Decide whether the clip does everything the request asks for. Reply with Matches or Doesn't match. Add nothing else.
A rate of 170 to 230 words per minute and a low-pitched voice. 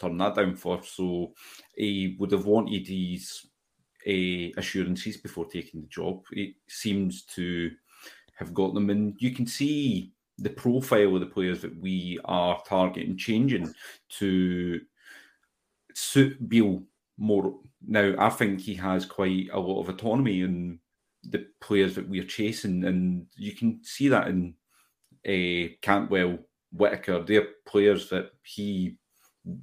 Doesn't match